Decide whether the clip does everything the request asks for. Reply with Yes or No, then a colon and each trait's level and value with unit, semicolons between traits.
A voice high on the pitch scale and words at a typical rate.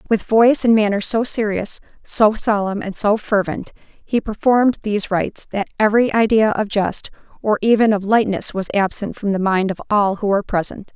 Yes: high, 210 Hz; average, 185 wpm